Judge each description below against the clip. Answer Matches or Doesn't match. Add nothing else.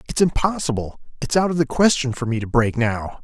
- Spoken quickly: Matches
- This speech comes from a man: Matches